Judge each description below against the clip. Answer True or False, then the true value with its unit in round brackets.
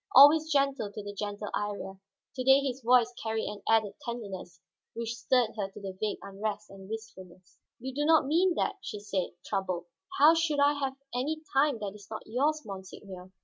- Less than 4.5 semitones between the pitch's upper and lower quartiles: False (5.5 semitones)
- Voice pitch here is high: True (225 Hz)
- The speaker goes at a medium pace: True (185 wpm)